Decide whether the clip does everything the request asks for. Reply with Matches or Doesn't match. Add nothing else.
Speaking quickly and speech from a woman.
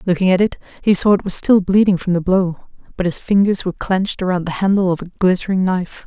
Matches